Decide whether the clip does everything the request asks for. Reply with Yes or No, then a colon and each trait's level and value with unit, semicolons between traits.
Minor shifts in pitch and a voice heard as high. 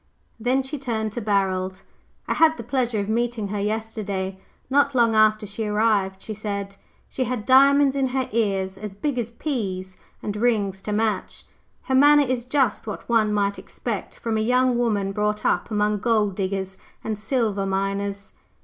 No: average, 3.5 semitones; high, 215 Hz